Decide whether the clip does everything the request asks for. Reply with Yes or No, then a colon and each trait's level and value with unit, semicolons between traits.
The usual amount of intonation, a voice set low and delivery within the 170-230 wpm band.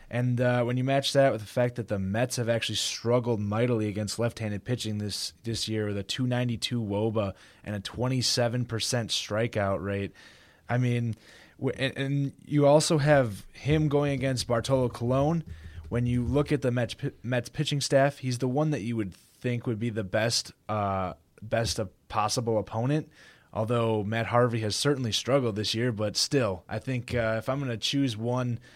Yes: average, 3.2 semitones; low, 120 Hz; average, 185 wpm